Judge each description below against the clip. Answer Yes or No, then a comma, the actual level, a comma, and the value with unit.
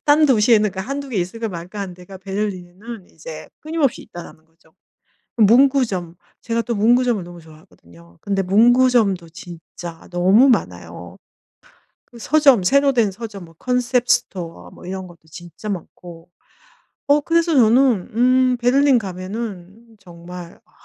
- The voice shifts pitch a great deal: Yes, wide, 5.9 semitones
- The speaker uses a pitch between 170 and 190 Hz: No, high, 205 Hz